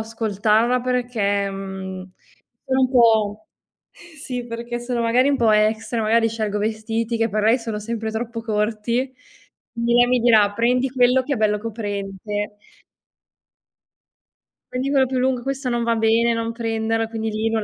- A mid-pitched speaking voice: No, high, 230 Hz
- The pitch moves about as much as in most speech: No, narrow, 2.2 semitones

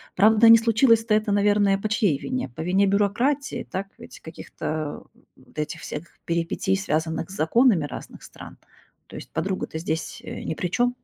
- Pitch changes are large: Yes, wide, 5.8 semitones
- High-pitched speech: Yes, high, 200 Hz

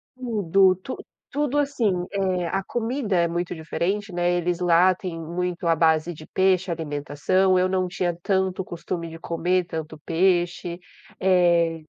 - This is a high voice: No, medium, 180 Hz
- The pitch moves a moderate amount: No, narrow, 2.2 semitones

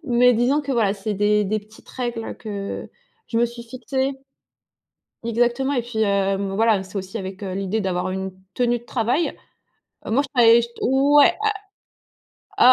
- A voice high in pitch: Yes, high, 230 Hz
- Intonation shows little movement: No, average, 3.7 semitones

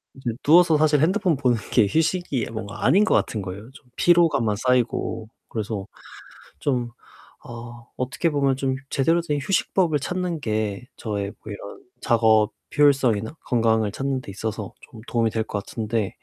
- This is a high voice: No, low, 120 Hz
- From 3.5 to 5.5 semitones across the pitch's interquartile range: Yes, average, 5.2 semitones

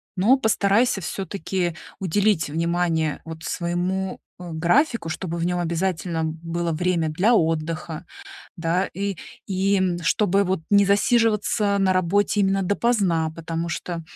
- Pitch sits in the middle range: Yes, medium, 180 Hz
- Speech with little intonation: No, average, 3.2 semitones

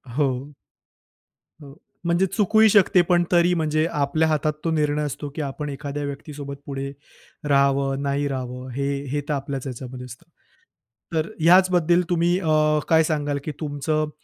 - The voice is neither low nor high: Yes, medium, 150 Hz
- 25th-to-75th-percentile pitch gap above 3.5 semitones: No, average, 3.0 semitones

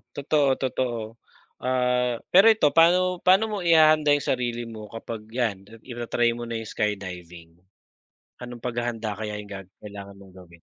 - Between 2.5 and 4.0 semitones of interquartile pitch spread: No, average, 4.5 semitones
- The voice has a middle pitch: No, low, 120 Hz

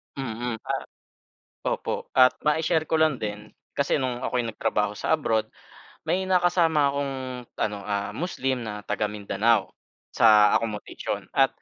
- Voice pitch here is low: Yes, low, 120 Hz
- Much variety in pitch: Yes, wide, 6.1 semitones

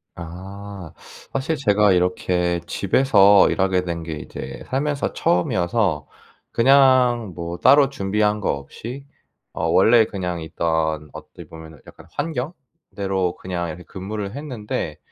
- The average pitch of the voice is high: No, very low, 95 Hz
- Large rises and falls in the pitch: Yes, wide, 5.7 semitones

